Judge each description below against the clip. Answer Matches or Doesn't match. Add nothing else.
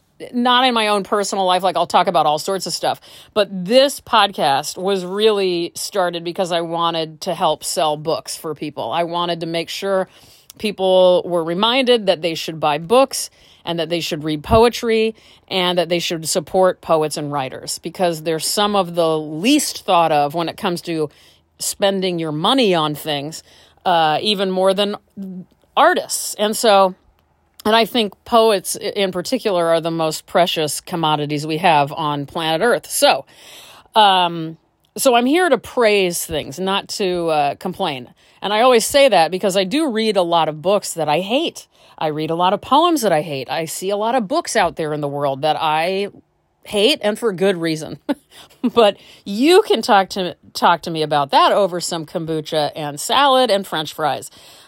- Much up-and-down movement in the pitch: Doesn't match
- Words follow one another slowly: Doesn't match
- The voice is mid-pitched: Matches